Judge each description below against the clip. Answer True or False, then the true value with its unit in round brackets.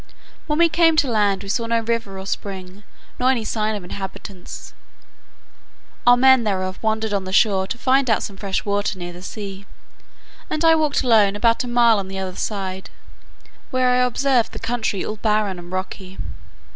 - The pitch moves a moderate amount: True (4.1 semitones)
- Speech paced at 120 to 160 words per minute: False (185 wpm)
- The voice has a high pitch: True (215 Hz)